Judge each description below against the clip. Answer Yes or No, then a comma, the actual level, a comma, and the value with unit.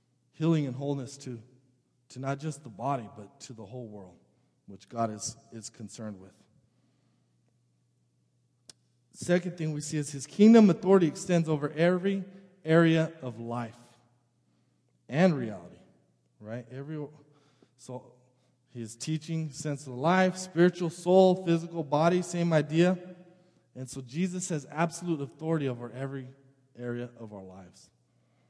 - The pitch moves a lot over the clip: Yes, wide, 5.9 semitones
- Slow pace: Yes, slow, 130 wpm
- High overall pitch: No, low, 135 Hz